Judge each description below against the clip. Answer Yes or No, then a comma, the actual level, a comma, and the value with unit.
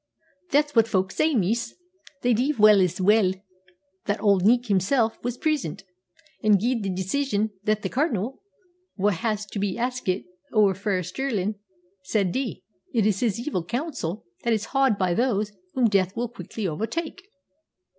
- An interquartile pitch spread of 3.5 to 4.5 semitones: Yes, average, 4.0 semitones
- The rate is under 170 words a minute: Yes, average, 160 wpm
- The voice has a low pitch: No, high, 215 Hz